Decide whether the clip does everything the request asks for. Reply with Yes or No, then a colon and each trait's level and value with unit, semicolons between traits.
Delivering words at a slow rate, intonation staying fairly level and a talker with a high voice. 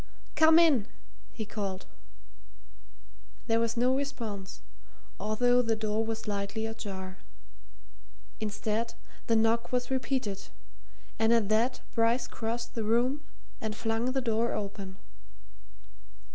Yes: slow, 115 wpm; narrow, 2.2 semitones; high, 225 Hz